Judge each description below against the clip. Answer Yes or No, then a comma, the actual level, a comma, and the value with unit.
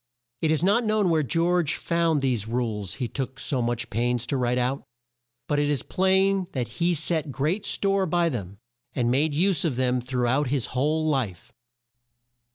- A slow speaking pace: No, average, 180 wpm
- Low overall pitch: No, medium, 145 Hz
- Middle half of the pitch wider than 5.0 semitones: Yes, wide, 5.4 semitones